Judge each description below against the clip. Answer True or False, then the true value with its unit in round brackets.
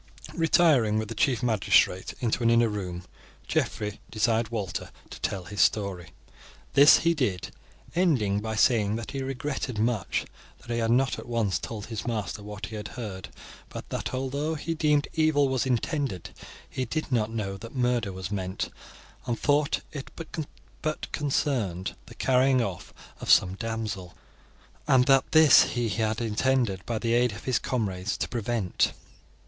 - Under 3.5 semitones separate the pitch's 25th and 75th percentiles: False (4.3 semitones)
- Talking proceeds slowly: False (165 wpm)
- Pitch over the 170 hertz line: False (115 Hz)